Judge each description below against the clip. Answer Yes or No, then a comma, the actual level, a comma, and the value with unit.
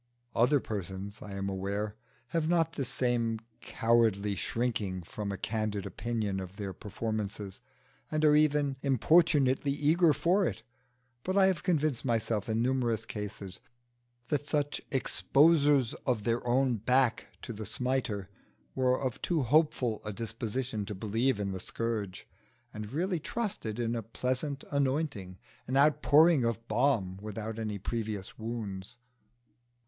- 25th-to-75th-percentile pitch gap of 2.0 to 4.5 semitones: No, average, 5.2 semitones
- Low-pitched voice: Yes, low, 115 Hz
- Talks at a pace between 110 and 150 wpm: Yes, average, 140 wpm